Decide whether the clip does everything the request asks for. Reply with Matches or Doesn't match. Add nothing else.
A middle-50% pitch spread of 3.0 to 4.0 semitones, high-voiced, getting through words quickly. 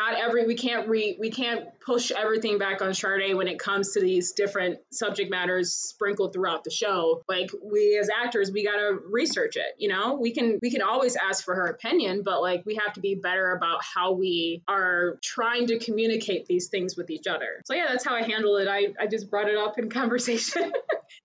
Matches